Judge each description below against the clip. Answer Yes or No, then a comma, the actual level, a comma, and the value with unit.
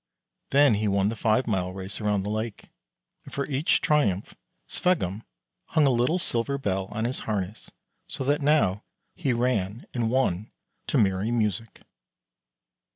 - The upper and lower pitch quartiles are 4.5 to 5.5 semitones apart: Yes, average, 4.9 semitones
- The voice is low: Yes, low, 110 Hz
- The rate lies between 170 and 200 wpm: No, average, 155 wpm